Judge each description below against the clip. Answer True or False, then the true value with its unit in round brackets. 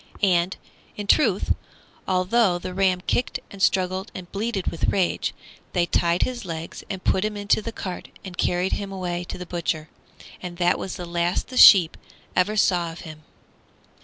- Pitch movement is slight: True (2.2 semitones)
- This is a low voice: False (185 Hz)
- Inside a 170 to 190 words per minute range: True (175 wpm)